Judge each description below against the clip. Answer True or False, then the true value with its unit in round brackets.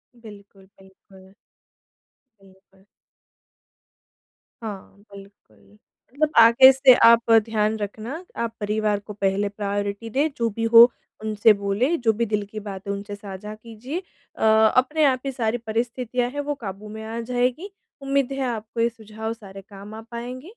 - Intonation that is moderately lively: True (3.2 semitones)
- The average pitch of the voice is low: False (220 Hz)